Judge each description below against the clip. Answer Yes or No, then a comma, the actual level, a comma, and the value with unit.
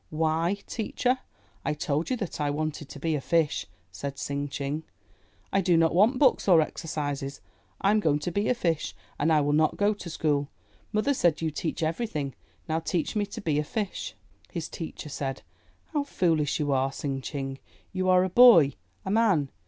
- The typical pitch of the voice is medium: Yes, medium, 160 Hz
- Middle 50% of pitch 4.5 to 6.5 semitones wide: Yes, average, 4.9 semitones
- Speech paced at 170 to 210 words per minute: Yes, average, 190 wpm